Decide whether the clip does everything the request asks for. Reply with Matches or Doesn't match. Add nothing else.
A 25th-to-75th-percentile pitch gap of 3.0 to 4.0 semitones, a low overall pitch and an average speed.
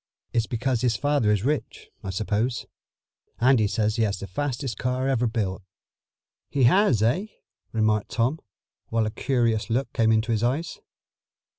Matches